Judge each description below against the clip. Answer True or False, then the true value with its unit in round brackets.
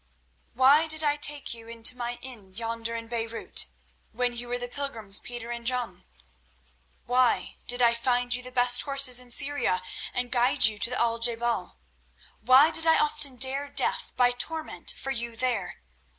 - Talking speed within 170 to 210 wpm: True (180 wpm)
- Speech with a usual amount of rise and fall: False (2.3 semitones)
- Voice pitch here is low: False (245 Hz)